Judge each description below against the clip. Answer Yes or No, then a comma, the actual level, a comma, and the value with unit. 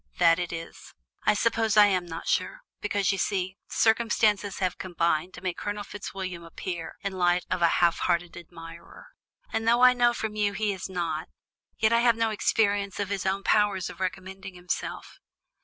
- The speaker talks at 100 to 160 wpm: No, average, 185 wpm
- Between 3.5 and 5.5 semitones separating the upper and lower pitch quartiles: No, average, 3.0 semitones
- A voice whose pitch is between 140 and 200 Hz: Yes, high, 190 Hz